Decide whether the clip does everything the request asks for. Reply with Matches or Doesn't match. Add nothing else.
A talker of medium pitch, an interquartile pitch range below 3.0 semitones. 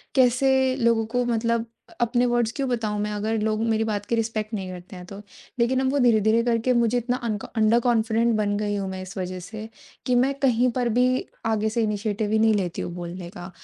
Doesn't match